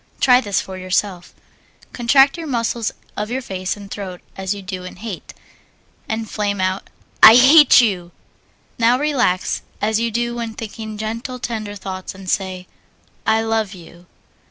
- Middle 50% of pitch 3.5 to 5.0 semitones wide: Yes, average, 3.9 semitones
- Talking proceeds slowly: No, average, 155 wpm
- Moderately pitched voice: No, high, 215 Hz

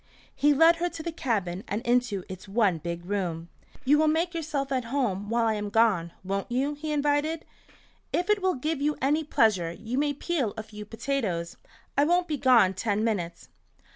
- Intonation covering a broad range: Yes, wide, 6.9 semitones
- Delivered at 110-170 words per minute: No, average, 195 wpm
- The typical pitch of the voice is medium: No, high, 240 Hz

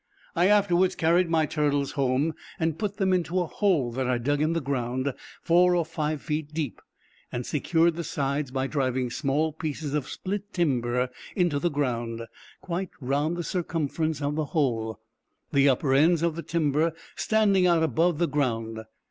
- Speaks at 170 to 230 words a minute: Yes, average, 175 wpm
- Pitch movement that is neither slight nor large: Yes, average, 3.9 semitones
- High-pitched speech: No, medium, 150 Hz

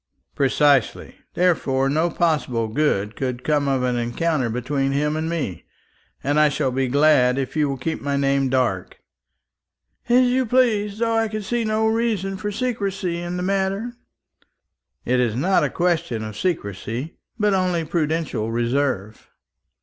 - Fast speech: No, average, 155 wpm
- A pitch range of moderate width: No, wide, 6.8 semitones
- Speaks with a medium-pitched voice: Yes, medium, 150 Hz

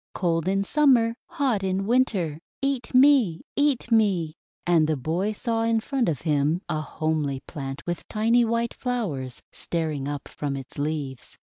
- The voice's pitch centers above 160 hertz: Yes, medium, 185 Hz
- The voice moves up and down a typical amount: No, wide, 7.2 semitones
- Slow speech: No, average, 155 wpm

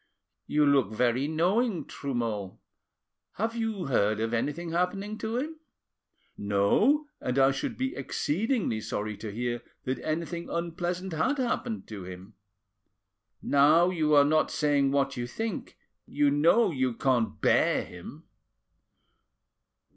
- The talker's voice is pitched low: No, medium, 145 Hz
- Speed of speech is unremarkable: No, slow, 130 wpm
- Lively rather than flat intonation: Yes, wide, 7.2 semitones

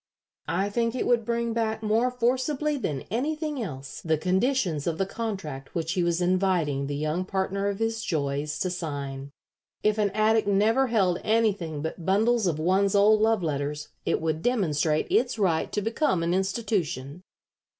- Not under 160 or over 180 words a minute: Yes, average, 170 wpm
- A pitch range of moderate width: No, wide, 5.9 semitones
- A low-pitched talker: No, high, 195 Hz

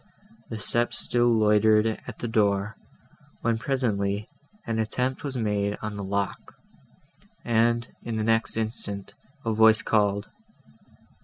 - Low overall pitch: Yes, low, 110 Hz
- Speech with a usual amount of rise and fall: No, narrow, 2.1 semitones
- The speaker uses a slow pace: Yes, slow, 130 wpm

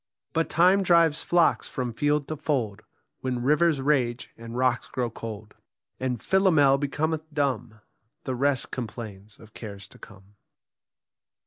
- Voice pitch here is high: No, low, 130 Hz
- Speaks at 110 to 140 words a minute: Yes, slow, 135 wpm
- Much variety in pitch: No, average, 4.8 semitones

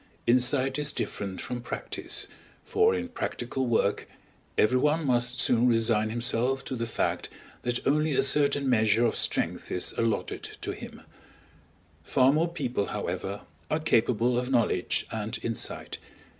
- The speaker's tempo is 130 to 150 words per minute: Yes, average, 140 wpm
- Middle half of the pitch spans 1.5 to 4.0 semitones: Yes, average, 3.3 semitones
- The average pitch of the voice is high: No, low, 125 Hz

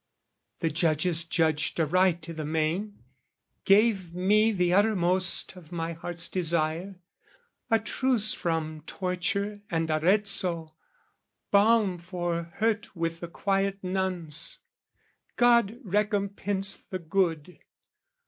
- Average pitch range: Yes, average, 3.3 semitones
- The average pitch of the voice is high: No, medium, 180 Hz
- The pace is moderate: No, slow, 105 wpm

